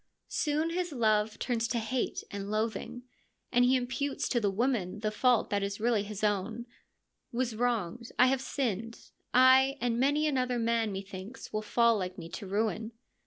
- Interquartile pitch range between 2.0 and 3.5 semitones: Yes, average, 3.2 semitones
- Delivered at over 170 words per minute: Yes, average, 180 wpm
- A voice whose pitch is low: No, high, 230 Hz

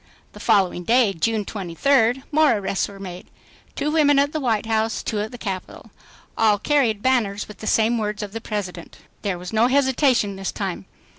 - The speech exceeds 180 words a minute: Yes, average, 190 wpm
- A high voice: Yes, high, 220 Hz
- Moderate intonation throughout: Yes, average, 4.3 semitones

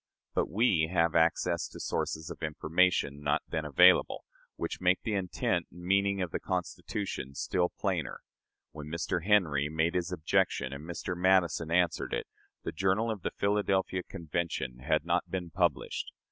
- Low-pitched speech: Yes, very low, 85 Hz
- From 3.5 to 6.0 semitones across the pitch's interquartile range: No, average, 3.0 semitones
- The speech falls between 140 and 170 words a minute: Yes, average, 160 wpm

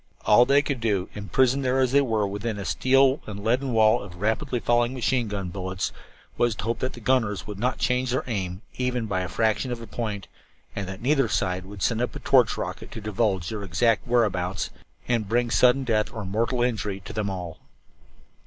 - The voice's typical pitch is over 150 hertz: No, low, 110 Hz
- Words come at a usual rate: No, fast, 210 wpm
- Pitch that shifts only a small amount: No, average, 3.8 semitones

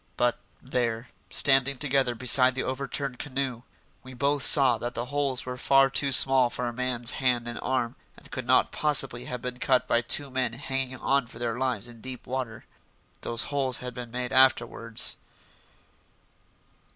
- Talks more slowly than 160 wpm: No, average, 175 wpm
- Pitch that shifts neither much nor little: No, narrow, 1.8 semitones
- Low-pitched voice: Yes, low, 130 Hz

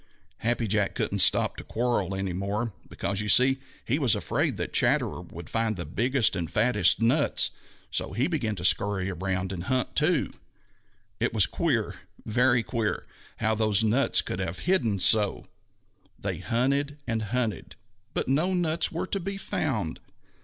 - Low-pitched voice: Yes, low, 110 Hz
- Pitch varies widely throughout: No, average, 4.8 semitones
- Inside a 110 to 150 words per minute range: No, average, 160 wpm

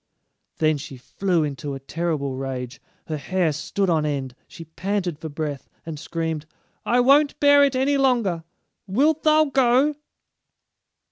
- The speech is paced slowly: No, average, 145 wpm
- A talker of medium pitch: Yes, medium, 170 Hz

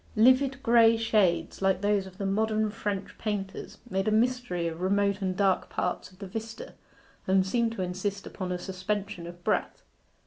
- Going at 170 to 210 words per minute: Yes, average, 180 wpm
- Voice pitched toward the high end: Yes, high, 200 Hz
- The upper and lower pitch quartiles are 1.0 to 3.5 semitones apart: Yes, average, 2.9 semitones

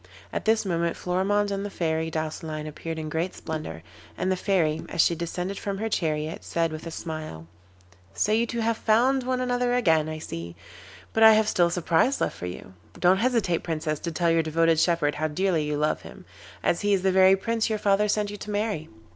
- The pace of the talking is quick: Yes, fast, 215 wpm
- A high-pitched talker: No, medium, 175 Hz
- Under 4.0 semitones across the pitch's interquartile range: No, average, 4.6 semitones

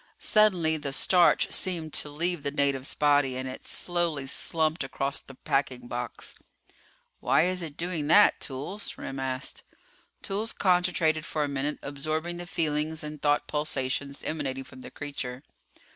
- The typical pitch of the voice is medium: Yes, medium, 150 Hz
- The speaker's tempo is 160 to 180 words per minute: No, average, 150 wpm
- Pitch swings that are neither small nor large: Yes, average, 3.8 semitones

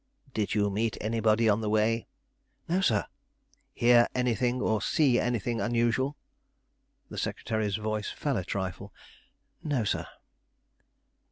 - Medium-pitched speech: No, low, 115 Hz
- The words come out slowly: Yes, slow, 125 wpm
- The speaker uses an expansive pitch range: No, narrow, 2.4 semitones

